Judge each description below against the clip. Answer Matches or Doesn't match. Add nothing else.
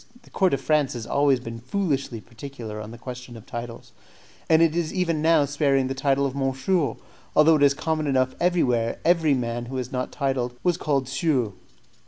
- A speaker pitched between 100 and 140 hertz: Matches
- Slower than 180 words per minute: Doesn't match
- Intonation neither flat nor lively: Matches